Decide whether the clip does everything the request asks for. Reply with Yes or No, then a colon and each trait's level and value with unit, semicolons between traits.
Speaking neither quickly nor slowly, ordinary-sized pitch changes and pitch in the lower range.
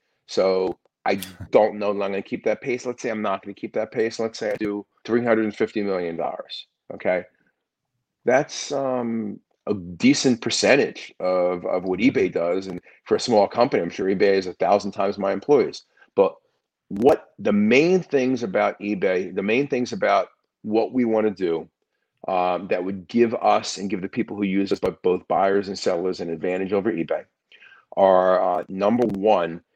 Yes: average, 185 wpm; average, 3.2 semitones; low, 100 Hz